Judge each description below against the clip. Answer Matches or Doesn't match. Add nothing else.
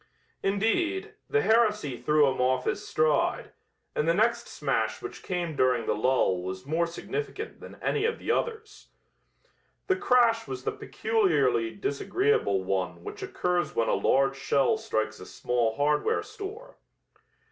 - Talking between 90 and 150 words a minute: Matches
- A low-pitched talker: Doesn't match